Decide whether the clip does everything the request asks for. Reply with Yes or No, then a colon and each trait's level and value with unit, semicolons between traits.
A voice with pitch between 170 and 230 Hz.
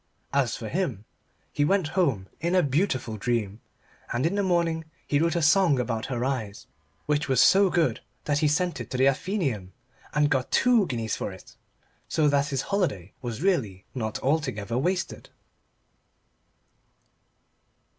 No: medium, 140 Hz